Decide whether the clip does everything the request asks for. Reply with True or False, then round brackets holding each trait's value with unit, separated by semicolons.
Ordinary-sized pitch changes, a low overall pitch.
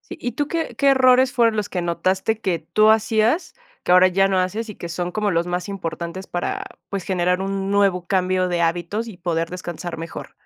False (3.4 semitones; 185 Hz)